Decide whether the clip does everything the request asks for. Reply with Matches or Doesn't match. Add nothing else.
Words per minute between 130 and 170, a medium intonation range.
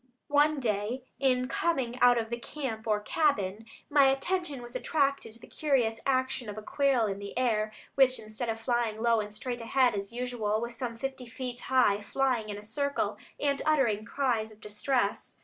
Doesn't match